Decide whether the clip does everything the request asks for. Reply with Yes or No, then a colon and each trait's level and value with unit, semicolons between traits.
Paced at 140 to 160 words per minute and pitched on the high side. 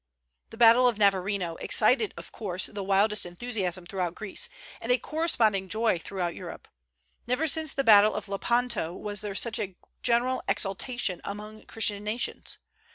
Yes: average, 155 wpm; high, 210 Hz